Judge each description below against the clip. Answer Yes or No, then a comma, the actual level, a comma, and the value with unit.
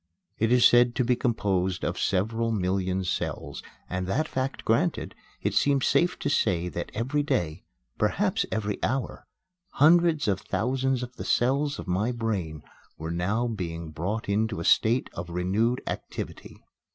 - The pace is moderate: Yes, average, 155 wpm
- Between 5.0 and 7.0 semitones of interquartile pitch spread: Yes, wide, 5.5 semitones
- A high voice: No, low, 110 Hz